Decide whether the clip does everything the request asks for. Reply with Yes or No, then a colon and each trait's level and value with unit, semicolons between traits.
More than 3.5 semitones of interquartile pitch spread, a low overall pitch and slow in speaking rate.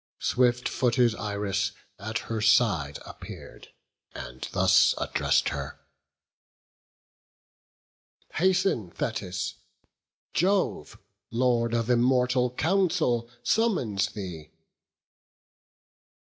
Yes: average, 4.0 semitones; low, 120 Hz; slow, 75 wpm